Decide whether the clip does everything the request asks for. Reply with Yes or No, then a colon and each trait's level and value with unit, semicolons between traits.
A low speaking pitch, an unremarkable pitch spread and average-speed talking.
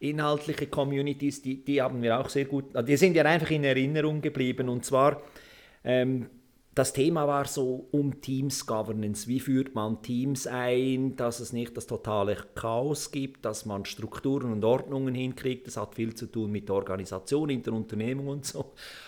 Yes: low, 130 Hz; average, 3.3 semitones; average, 175 wpm